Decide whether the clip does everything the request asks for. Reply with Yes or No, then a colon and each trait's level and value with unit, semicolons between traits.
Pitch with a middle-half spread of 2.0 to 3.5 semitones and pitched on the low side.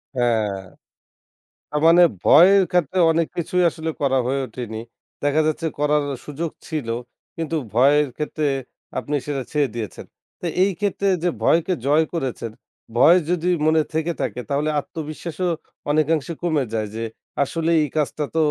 No: average, 3.2 semitones; medium, 155 Hz